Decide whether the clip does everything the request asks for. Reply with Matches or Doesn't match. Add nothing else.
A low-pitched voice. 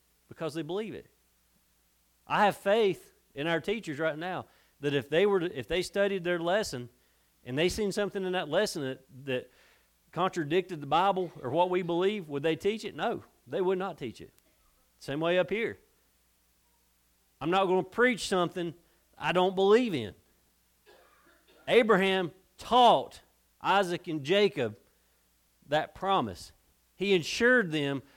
Doesn't match